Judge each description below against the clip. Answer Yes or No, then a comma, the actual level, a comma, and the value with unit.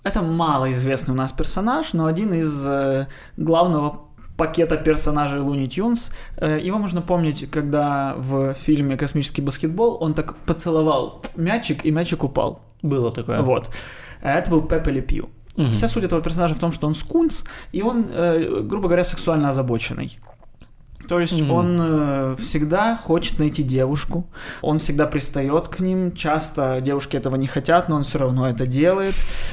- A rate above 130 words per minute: Yes, average, 150 wpm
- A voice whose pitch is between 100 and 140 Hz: No, medium, 155 Hz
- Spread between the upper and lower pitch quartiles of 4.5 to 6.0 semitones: No, average, 3.5 semitones